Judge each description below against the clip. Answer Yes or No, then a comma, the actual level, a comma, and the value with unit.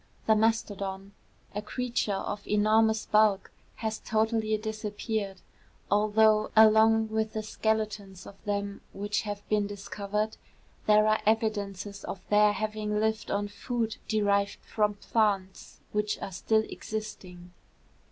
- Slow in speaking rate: Yes, slow, 125 wpm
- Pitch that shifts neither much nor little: No, narrow, 1.3 semitones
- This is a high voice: Yes, high, 210 Hz